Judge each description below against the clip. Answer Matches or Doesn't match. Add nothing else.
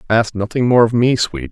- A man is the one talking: Matches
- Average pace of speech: Doesn't match